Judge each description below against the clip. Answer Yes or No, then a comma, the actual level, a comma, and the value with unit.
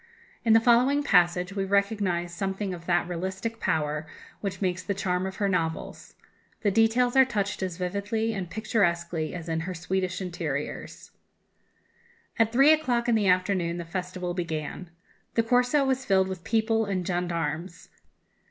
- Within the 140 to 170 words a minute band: Yes, average, 155 wpm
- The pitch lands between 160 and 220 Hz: Yes, high, 190 Hz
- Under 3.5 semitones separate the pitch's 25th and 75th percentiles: No, average, 4.1 semitones